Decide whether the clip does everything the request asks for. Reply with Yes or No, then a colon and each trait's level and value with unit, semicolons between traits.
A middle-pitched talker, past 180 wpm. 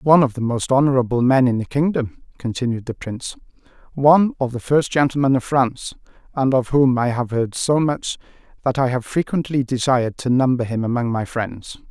No: low, 130 Hz; average, 190 wpm